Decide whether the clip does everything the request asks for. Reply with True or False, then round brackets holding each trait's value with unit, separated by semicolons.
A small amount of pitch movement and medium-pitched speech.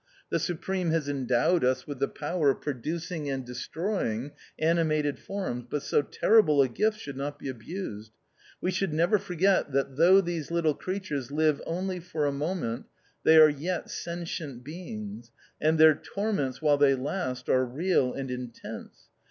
False (4.6 semitones; 150 Hz)